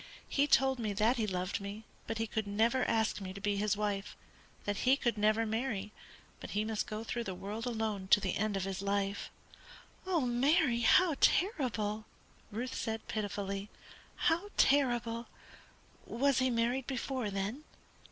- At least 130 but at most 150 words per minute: No, average, 160 wpm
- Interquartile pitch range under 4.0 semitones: Yes, average, 3.6 semitones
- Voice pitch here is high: Yes, high, 220 Hz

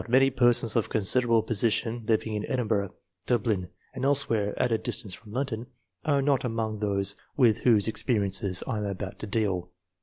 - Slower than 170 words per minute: No, average, 175 wpm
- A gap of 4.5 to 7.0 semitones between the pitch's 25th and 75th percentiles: No, average, 3.1 semitones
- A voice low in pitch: Yes, low, 110 Hz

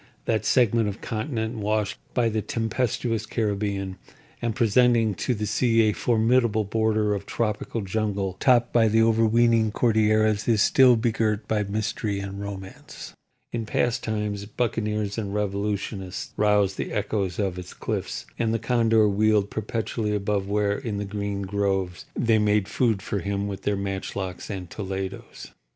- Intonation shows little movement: Yes, narrow, 2.1 semitones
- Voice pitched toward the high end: No, low, 105 Hz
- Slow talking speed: No, average, 150 wpm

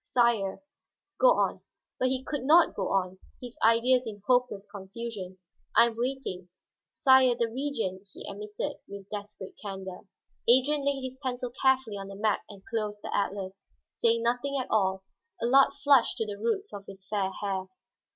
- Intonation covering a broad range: No, average, 4.6 semitones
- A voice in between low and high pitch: No, high, 225 Hz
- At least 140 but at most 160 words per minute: No, average, 170 wpm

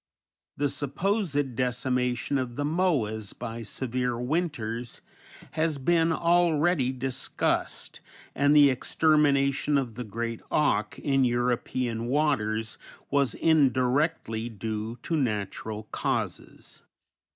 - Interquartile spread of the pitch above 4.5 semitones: No, average, 4.2 semitones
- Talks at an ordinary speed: No, slow, 100 wpm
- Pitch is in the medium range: No, low, 130 Hz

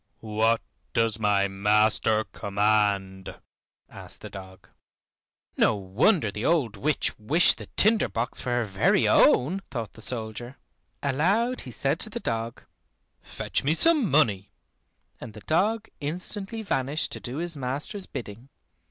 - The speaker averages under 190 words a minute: Yes, average, 140 wpm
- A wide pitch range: Yes, wide, 7.2 semitones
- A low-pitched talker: Yes, low, 120 Hz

